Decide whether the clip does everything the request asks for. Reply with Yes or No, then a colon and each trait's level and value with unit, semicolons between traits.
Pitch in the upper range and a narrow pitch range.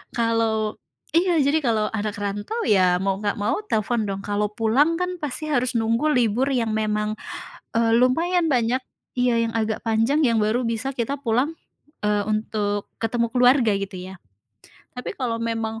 No: high, 230 Hz; average, 3.0 semitones